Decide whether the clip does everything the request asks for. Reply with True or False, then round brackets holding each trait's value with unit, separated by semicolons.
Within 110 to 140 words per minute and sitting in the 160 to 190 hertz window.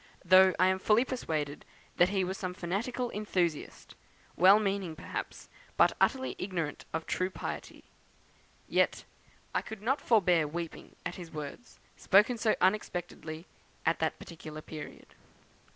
True (135 wpm; 185 Hz)